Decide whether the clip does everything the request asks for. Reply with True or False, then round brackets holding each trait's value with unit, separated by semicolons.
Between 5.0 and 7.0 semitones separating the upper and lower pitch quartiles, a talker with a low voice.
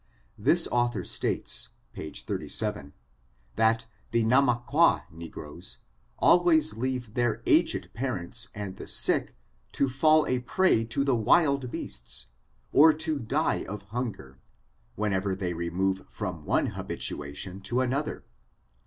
True (5.6 semitones; 115 Hz)